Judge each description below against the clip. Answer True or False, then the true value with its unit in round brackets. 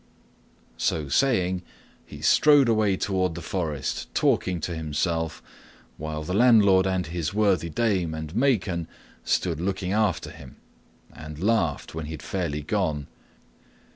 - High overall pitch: False (90 Hz)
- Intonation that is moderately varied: True (4.2 semitones)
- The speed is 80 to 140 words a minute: True (135 wpm)